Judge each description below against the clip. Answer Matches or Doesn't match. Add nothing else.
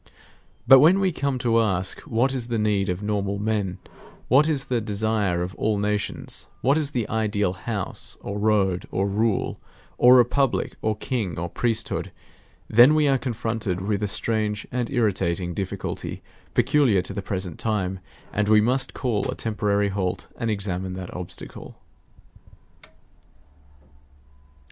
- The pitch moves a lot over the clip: Doesn't match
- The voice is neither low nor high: Doesn't match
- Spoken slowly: Doesn't match